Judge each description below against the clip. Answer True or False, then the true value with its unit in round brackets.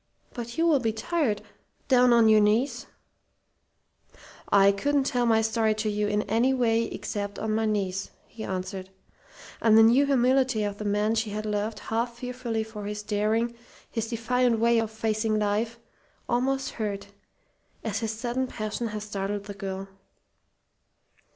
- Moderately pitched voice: False (220 Hz)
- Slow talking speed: False (160 wpm)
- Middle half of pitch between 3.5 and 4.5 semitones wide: False (2.4 semitones)